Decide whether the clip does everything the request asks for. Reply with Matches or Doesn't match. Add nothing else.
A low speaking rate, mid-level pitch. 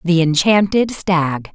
Matches